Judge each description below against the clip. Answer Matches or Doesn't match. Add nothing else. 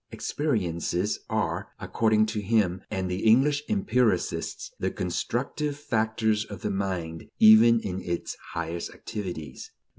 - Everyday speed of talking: Doesn't match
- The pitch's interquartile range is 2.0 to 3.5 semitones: Doesn't match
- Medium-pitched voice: Doesn't match